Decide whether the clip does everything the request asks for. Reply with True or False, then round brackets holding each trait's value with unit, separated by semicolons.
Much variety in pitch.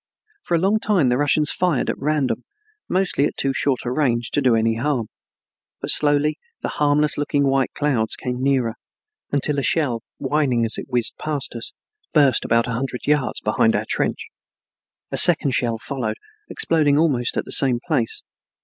False (3.5 semitones)